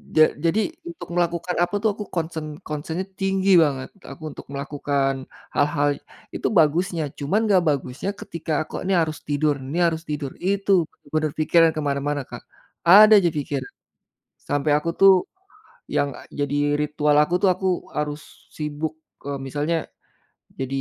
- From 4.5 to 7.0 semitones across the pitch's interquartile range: No, average, 3.3 semitones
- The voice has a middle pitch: Yes, medium, 155 Hz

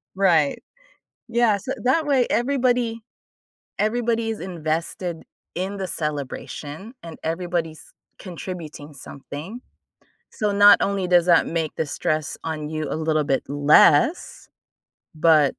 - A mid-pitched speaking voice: Yes, medium, 175 Hz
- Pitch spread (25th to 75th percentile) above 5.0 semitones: Yes, wide, 5.5 semitones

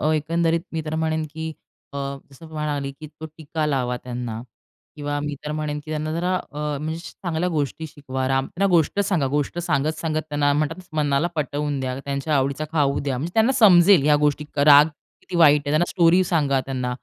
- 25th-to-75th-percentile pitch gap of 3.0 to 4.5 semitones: No, narrow, 2.5 semitones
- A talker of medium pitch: Yes, medium, 150 Hz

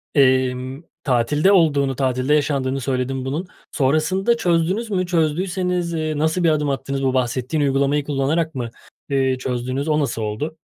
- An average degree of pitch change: Yes, average, 3.7 semitones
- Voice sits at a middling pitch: Yes, medium, 145 Hz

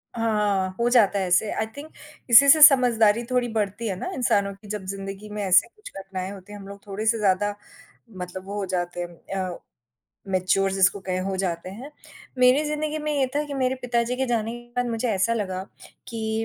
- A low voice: No, high, 210 Hz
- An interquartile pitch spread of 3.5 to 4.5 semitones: Yes, average, 3.8 semitones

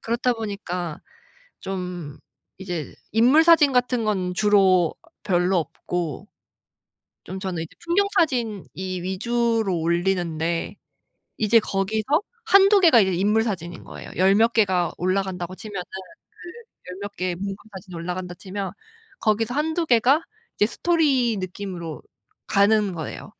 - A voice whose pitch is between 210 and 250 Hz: No, high, 195 Hz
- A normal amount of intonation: Yes, average, 4.5 semitones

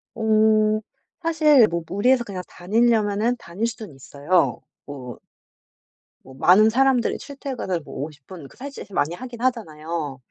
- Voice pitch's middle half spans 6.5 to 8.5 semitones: Yes, wide, 6.9 semitones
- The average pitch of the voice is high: Yes, high, 210 Hz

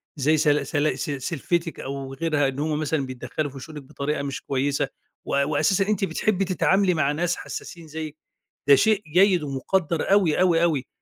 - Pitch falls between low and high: Yes, medium, 155 Hz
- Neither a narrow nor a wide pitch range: Yes, average, 3.8 semitones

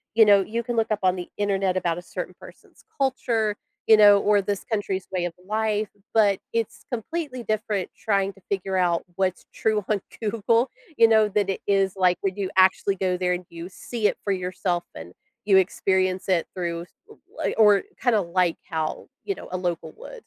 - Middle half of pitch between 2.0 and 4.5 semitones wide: Yes, average, 2.9 semitones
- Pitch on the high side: Yes, high, 195 Hz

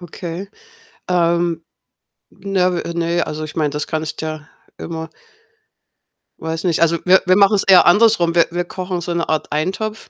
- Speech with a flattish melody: Yes, narrow, 2.3 semitones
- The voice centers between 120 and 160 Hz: No, medium, 170 Hz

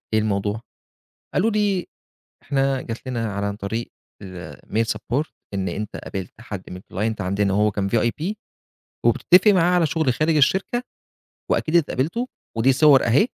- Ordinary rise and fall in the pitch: No, wide, 7.6 semitones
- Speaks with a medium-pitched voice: No, low, 120 Hz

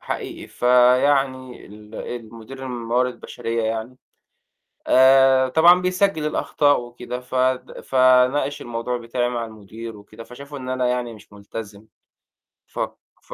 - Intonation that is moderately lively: No, narrow, 2.3 semitones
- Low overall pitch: Yes, low, 125 Hz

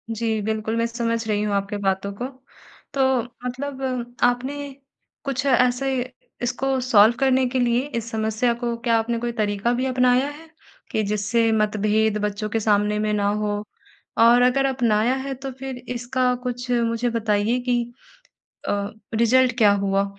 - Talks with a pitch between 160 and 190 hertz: No, high, 235 Hz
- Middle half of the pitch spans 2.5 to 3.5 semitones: Yes, average, 3.0 semitones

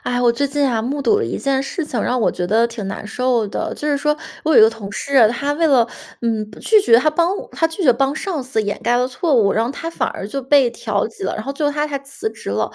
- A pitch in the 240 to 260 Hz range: Yes, very high, 255 Hz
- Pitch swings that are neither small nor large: Yes, average, 4.3 semitones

